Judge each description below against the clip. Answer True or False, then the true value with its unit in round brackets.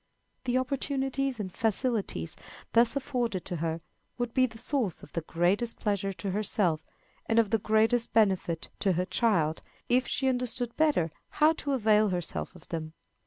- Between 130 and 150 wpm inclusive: False (165 wpm)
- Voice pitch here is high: True (220 Hz)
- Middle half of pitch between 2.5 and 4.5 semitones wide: False (5.6 semitones)